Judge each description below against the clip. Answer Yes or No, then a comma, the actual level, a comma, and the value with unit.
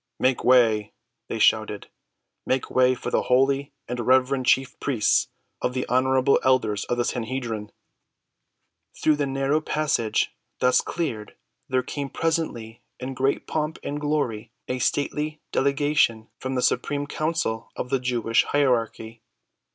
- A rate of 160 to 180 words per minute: No, slow, 135 wpm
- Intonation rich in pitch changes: No, average, 3.0 semitones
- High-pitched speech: No, low, 130 Hz